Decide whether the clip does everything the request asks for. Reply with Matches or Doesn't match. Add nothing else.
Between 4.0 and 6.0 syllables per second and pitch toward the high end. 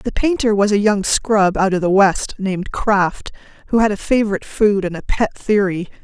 Matches